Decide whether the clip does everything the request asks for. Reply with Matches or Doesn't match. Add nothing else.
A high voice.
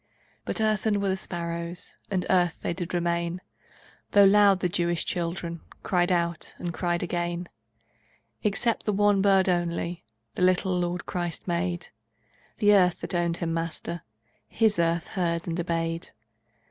Doesn't match